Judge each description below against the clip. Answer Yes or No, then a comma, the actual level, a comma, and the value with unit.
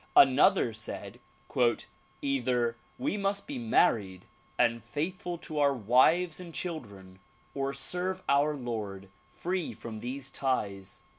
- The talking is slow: Yes, slow, 120 wpm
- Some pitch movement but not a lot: No, wide, 7.2 semitones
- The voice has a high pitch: No, low, 135 Hz